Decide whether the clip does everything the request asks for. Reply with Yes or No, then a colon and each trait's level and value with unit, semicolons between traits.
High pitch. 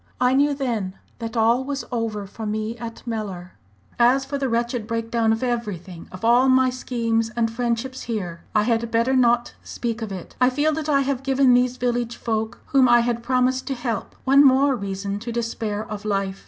Yes: high, 235 Hz